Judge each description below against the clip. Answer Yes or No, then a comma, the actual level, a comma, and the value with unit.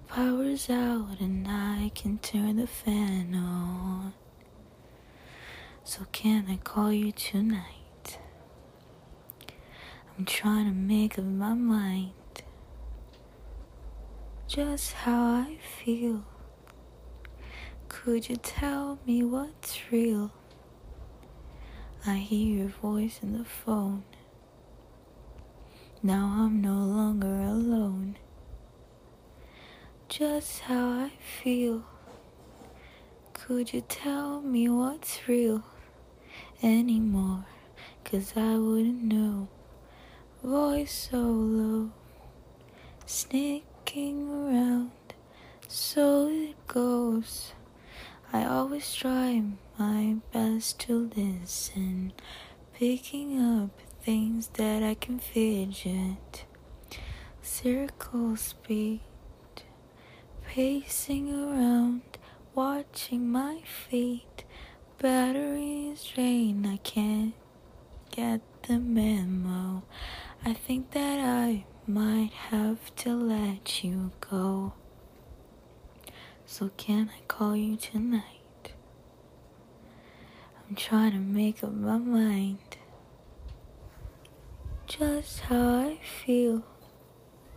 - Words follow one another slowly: Yes, slow, 85 wpm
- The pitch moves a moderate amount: Yes, average, 3.8 semitones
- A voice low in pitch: No, high, 220 Hz